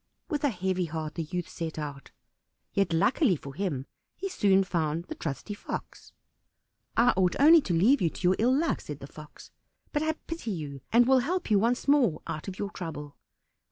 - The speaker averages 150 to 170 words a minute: No, average, 195 wpm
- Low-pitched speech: No, medium, 185 Hz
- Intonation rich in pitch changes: Yes, wide, 7.8 semitones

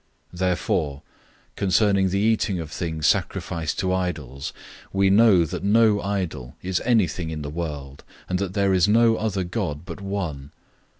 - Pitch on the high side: No, very low, 95 Hz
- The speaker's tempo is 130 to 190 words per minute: Yes, average, 160 wpm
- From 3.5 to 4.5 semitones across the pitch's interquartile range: Yes, average, 4.0 semitones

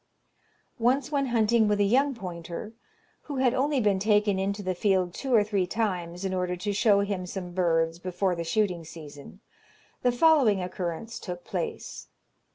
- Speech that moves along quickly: No, average, 165 wpm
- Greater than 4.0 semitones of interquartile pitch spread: Yes, average, 4.4 semitones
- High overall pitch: Yes, high, 200 Hz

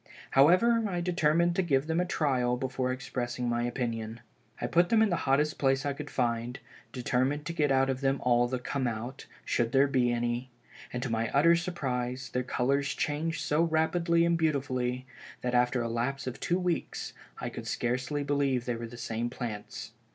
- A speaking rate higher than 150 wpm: Yes, average, 190 wpm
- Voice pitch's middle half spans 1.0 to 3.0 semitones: No, average, 3.8 semitones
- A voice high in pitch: No, low, 135 Hz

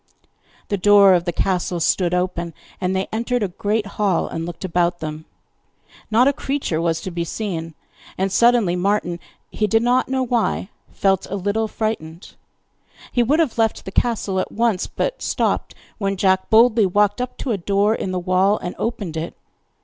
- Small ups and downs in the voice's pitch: No, average, 3.9 semitones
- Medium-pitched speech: No, high, 195 Hz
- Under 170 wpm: No, average, 180 wpm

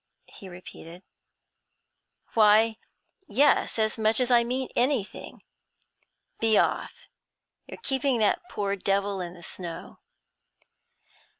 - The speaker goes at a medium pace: No, slow, 105 wpm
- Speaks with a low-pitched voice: No, high, 215 Hz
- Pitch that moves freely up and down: No, average, 3.5 semitones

